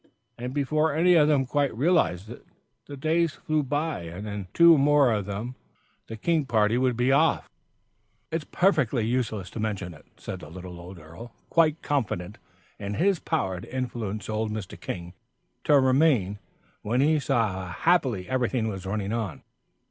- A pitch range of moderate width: No, wide, 6.5 semitones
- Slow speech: No, average, 170 wpm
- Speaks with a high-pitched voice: No, low, 120 Hz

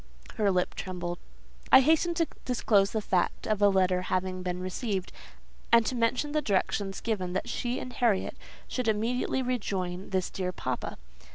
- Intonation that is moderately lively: Yes, average, 4.7 semitones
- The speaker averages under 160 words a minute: No, average, 165 wpm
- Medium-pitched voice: No, high, 205 Hz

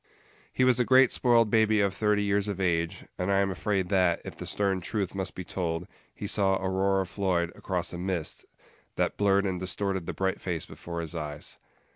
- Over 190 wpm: Yes, average, 200 wpm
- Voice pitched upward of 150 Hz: No, very low, 95 Hz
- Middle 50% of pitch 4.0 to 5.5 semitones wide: No, narrow, 2.4 semitones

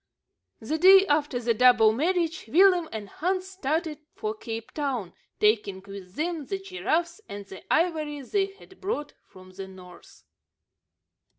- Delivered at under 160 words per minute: Yes, average, 140 wpm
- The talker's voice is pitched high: Yes, very high, 295 Hz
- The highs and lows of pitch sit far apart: Yes, wide, 8.8 semitones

